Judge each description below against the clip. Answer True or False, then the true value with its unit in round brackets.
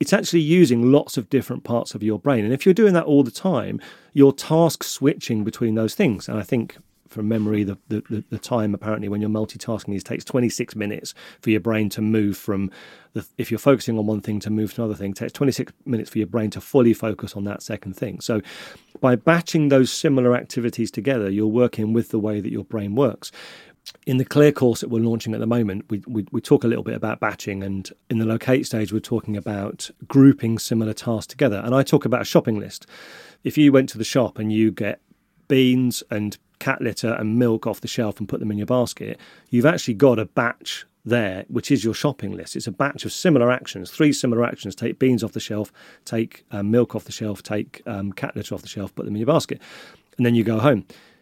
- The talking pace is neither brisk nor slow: False (235 wpm)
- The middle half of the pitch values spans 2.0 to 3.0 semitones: False (3.5 semitones)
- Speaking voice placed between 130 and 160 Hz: False (115 Hz)